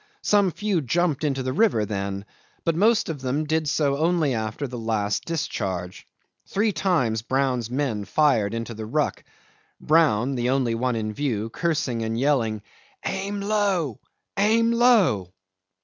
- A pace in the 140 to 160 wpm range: Yes, average, 150 wpm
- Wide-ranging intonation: Yes, wide, 7.1 semitones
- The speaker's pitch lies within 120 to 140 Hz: Yes, low, 135 Hz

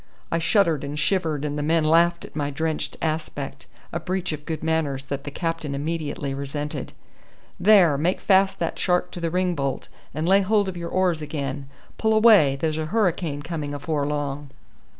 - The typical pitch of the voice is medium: Yes, medium, 160 Hz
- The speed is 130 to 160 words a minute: No, average, 185 wpm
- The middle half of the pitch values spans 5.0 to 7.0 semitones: No, average, 3.4 semitones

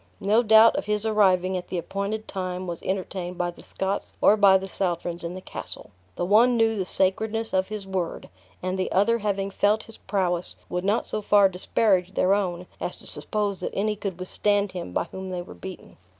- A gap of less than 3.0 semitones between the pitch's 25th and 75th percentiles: Yes, narrow, 2.4 semitones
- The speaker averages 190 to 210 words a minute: Yes, fast, 205 wpm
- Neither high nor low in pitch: No, high, 195 Hz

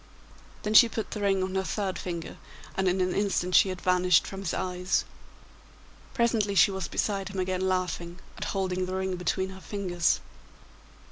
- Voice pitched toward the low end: No, high, 190 Hz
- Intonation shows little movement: Yes, narrow, 1.3 semitones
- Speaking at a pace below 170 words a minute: No, average, 180 wpm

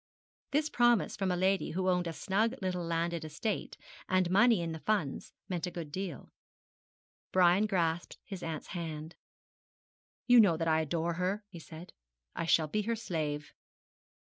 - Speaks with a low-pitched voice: No, medium, 180 Hz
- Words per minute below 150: No, average, 165 wpm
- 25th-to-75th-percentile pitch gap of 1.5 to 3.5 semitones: Yes, average, 3.2 semitones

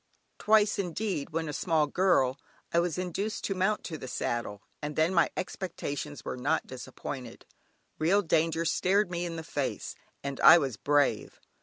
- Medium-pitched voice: Yes, medium, 165 Hz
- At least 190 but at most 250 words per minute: No, average, 165 wpm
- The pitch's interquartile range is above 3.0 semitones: Yes, average, 4.3 semitones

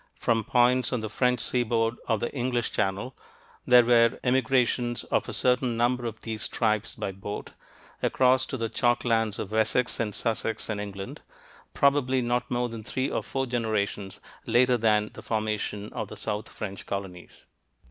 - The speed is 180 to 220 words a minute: No, average, 170 wpm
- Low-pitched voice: Yes, low, 115 Hz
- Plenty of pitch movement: No, narrow, 2.5 semitones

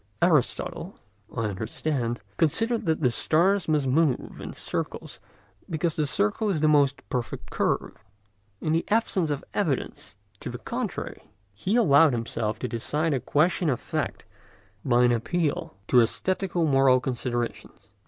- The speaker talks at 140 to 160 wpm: Yes, average, 145 wpm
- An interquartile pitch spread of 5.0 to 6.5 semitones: Yes, wide, 5.4 semitones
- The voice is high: No, medium, 150 Hz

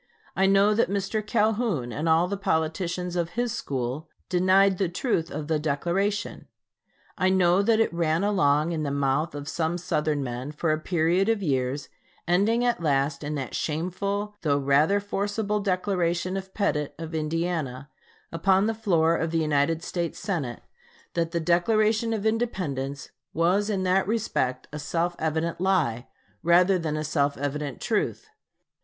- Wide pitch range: No, average, 4.5 semitones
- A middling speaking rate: Yes, average, 160 wpm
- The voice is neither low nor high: Yes, medium, 170 Hz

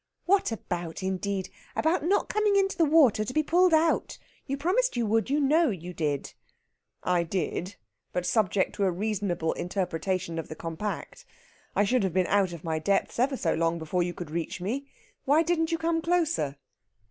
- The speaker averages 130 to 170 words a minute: No, average, 185 wpm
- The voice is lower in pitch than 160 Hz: No, high, 205 Hz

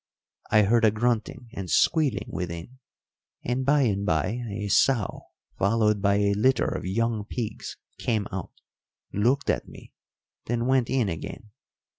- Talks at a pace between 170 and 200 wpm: No, average, 145 wpm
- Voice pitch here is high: No, low, 110 Hz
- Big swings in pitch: No, average, 3.5 semitones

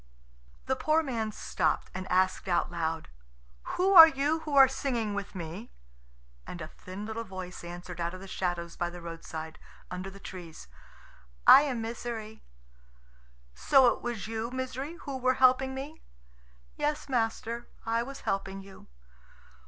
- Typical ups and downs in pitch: No, wide, 6.4 semitones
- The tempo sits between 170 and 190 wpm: No, average, 155 wpm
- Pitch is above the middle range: Yes, high, 220 Hz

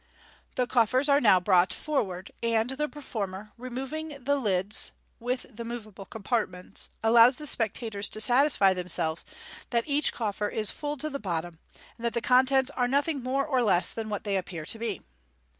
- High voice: Yes, high, 230 Hz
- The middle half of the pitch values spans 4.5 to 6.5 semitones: Yes, average, 4.9 semitones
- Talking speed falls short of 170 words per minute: No, average, 175 wpm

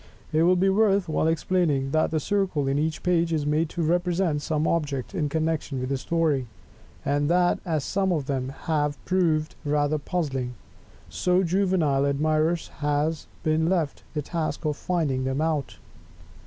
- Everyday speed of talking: Yes, average, 165 wpm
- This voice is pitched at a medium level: Yes, medium, 155 Hz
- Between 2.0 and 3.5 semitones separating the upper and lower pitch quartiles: Yes, average, 3.0 semitones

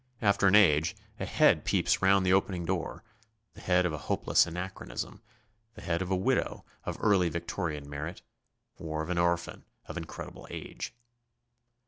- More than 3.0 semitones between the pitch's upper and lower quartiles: No, narrow, 2.6 semitones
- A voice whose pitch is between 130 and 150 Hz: No, very low, 90 Hz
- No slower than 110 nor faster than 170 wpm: Yes, average, 160 wpm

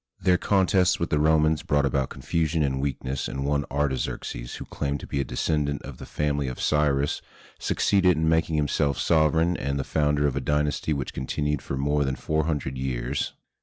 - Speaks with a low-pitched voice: Yes, very low, 75 Hz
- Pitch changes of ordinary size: No, narrow, 2.2 semitones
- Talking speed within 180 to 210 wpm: Yes, average, 190 wpm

